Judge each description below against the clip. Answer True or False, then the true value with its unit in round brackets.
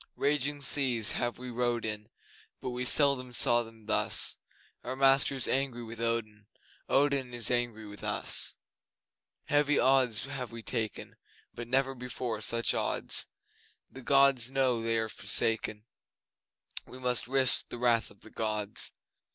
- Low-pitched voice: True (120 Hz)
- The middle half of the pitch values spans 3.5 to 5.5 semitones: False (2.8 semitones)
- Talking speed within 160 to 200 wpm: False (145 wpm)